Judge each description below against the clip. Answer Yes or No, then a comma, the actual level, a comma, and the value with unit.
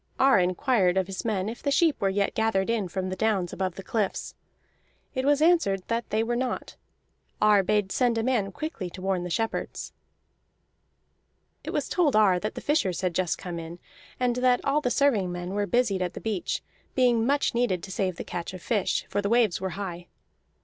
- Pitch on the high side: Yes, high, 205 Hz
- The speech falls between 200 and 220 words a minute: Yes, fast, 205 wpm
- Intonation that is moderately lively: Yes, average, 4.6 semitones